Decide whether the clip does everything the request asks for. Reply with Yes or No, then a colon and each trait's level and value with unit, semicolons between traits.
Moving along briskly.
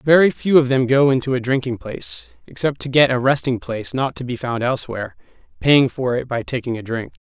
Yes: fast, 225 wpm